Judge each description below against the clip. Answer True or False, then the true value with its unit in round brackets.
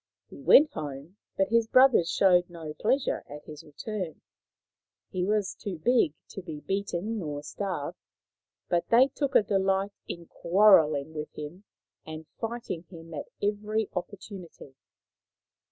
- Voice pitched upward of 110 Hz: True (185 Hz)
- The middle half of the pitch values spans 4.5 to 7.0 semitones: True (5.0 semitones)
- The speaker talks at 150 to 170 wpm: False (140 wpm)